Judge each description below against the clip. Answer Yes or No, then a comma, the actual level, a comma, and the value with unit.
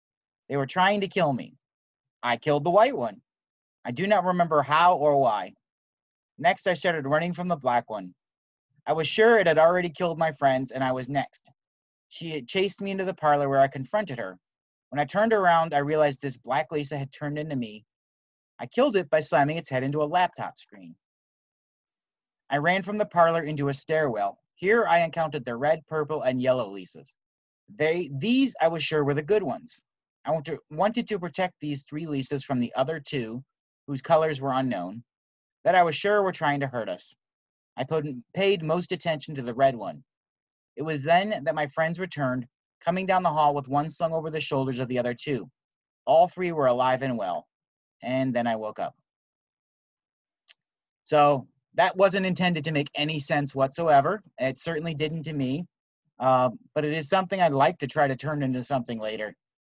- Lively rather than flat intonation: No, average, 4.5 semitones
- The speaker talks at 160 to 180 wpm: No, average, 195 wpm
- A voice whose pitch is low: No, medium, 150 Hz